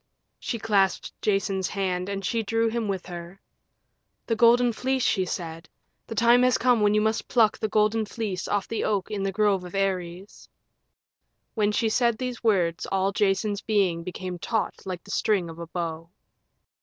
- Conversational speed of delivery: Yes, average, 180 wpm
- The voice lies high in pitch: Yes, high, 200 Hz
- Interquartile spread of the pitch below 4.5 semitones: Yes, average, 3.3 semitones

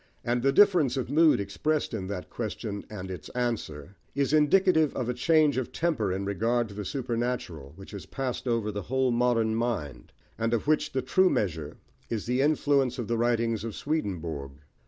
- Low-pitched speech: Yes, low, 120 Hz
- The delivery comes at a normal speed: Yes, average, 185 wpm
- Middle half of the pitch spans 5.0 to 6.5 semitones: Yes, average, 5.3 semitones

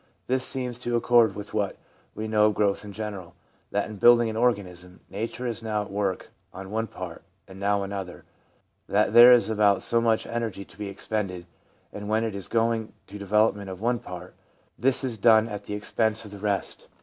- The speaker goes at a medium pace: No, fast, 210 wpm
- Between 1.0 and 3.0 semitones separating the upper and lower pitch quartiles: Yes, narrow, 2.5 semitones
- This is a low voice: Yes, low, 105 Hz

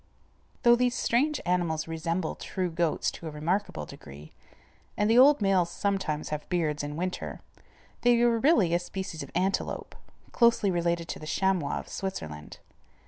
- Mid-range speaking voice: Yes, medium, 180 Hz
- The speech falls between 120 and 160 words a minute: Yes, average, 155 wpm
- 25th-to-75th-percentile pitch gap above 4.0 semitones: Yes, average, 4.5 semitones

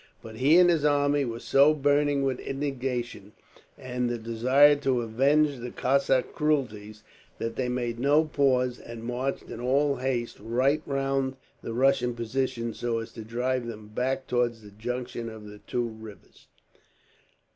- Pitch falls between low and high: No, low, 125 Hz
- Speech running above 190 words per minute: No, average, 155 wpm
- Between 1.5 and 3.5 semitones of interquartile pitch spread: Yes, average, 2.9 semitones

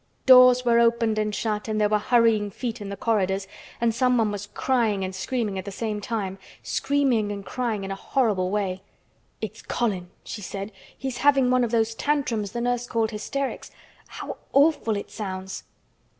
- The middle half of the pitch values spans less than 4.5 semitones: Yes, average, 3.3 semitones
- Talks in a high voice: Yes, high, 220 Hz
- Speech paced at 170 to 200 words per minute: Yes, average, 180 wpm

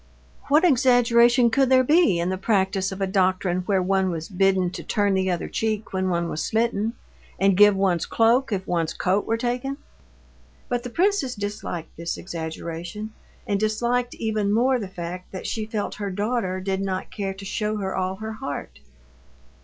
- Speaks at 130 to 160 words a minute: No, average, 180 wpm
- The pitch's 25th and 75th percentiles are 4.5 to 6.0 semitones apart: No, average, 3.7 semitones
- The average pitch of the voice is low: No, high, 200 Hz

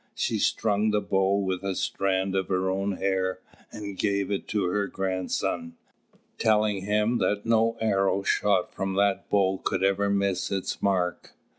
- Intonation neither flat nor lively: No, narrow, 1.4 semitones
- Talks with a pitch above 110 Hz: No, low, 100 Hz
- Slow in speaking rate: No, average, 160 wpm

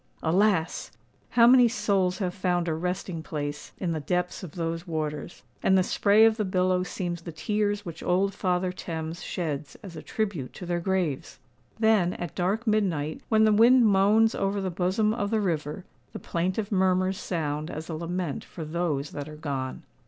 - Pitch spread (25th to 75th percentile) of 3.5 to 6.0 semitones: Yes, average, 3.8 semitones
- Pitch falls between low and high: Yes, medium, 180 Hz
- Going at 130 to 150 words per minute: No, average, 180 wpm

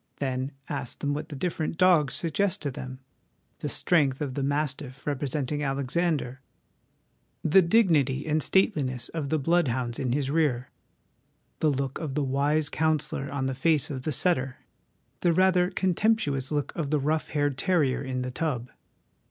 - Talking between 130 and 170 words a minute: Yes, average, 160 wpm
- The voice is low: No, medium, 145 Hz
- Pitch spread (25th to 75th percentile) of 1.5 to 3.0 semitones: No, average, 3.4 semitones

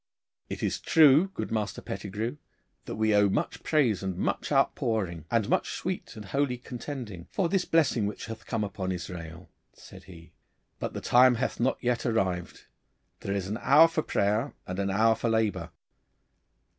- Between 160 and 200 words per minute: Yes, average, 170 wpm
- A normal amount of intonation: Yes, average, 4.7 semitones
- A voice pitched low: Yes, low, 110 Hz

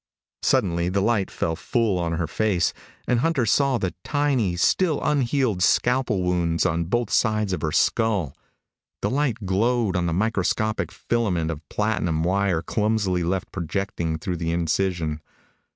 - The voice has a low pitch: Yes, very low, 95 Hz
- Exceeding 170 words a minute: No, average, 150 wpm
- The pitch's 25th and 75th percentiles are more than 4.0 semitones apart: Yes, average, 5.2 semitones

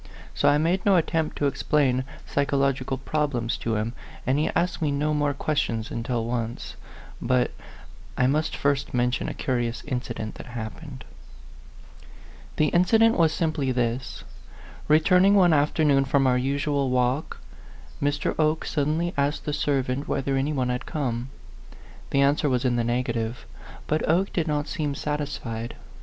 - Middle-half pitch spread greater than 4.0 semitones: No, average, 3.4 semitones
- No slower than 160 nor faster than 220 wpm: No, average, 150 wpm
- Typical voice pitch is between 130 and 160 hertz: Yes, medium, 140 Hz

